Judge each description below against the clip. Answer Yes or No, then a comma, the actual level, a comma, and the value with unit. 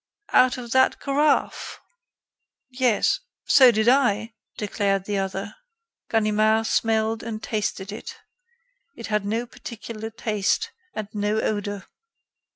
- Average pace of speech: No, slow, 115 wpm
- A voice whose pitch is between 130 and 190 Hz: No, high, 220 Hz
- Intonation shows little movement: Yes, narrow, 2.3 semitones